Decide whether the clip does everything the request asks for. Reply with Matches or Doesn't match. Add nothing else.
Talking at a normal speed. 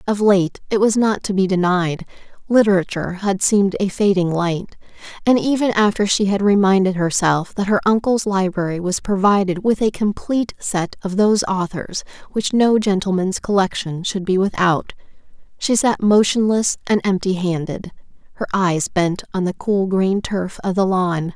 Matches